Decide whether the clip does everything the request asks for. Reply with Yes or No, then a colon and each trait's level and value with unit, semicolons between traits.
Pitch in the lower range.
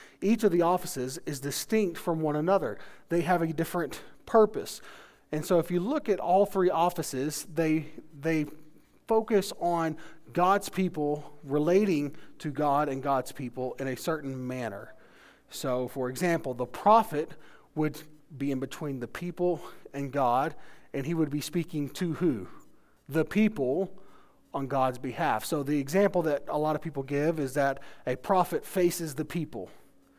No: medium, 155 Hz